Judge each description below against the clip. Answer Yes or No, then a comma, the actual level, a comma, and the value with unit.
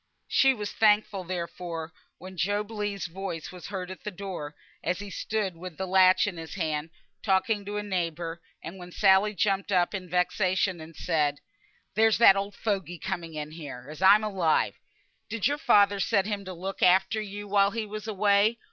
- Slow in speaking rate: No, average, 185 wpm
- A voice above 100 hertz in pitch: Yes, high, 190 Hz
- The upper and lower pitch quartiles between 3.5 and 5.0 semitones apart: No, average, 2.9 semitones